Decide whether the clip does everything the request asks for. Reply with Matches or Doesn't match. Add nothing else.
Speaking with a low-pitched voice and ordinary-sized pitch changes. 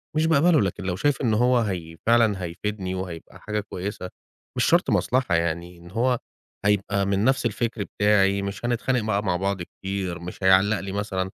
Matches